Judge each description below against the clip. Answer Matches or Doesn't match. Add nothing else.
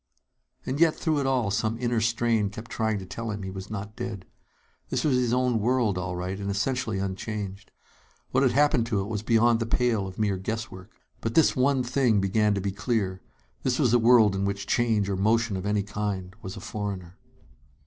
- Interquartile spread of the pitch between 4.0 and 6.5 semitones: Doesn't match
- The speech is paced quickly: Matches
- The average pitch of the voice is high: Doesn't match